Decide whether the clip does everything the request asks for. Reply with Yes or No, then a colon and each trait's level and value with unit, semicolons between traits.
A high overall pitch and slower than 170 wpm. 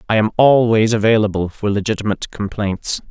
No: low, 105 Hz; slow, 135 wpm